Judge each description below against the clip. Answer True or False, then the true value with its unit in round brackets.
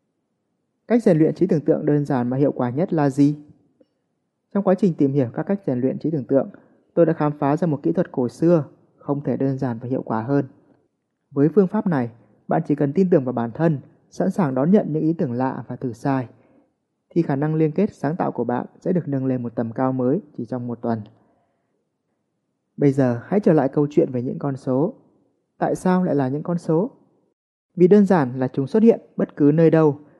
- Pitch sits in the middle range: True (145 Hz)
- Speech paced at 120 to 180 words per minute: False (235 wpm)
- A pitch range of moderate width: True (4.8 semitones)